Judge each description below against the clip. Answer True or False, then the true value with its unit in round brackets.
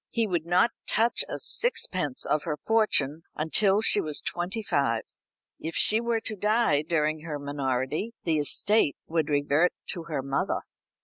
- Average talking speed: True (160 wpm)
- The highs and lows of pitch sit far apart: True (6.4 semitones)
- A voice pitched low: False (165 Hz)